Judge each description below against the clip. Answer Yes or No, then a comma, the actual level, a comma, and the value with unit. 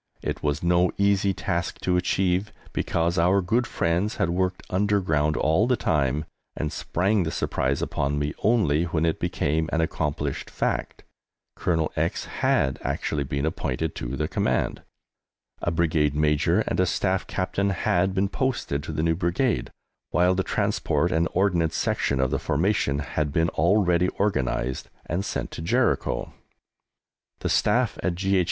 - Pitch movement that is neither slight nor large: Yes, average, 4.0 semitones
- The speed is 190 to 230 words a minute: No, average, 155 wpm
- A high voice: No, very low, 85 Hz